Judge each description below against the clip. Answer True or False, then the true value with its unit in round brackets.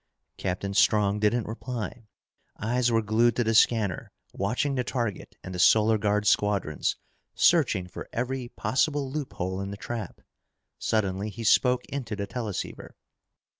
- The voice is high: False (110 Hz)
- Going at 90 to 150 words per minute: True (140 wpm)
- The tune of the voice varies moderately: True (3.4 semitones)